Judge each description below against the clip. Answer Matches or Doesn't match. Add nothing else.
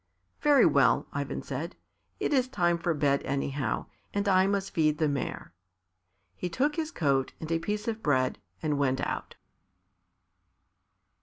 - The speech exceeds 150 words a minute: Doesn't match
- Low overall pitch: Doesn't match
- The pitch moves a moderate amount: Doesn't match